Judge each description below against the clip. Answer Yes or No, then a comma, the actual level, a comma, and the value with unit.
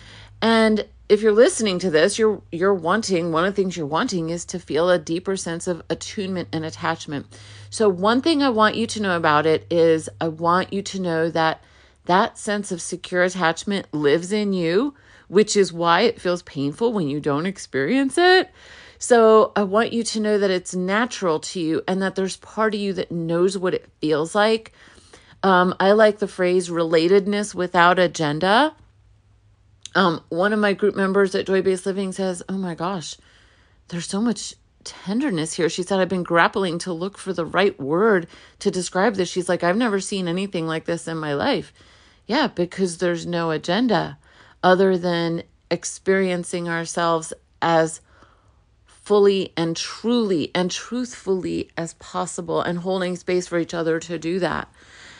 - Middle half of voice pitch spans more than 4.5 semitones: No, average, 3.3 semitones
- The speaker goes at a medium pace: Yes, average, 175 wpm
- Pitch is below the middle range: No, medium, 180 Hz